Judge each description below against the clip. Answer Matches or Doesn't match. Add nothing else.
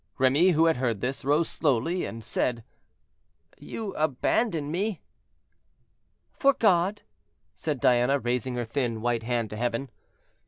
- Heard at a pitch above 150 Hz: Doesn't match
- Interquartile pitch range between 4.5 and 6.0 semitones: Matches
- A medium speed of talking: Doesn't match